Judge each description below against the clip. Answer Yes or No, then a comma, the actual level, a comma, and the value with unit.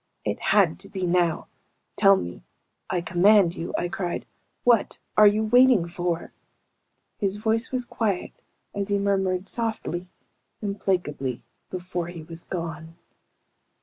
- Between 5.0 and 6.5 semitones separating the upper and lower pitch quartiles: No, average, 3.2 semitones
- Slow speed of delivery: Yes, slow, 130 wpm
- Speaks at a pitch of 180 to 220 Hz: Yes, high, 190 Hz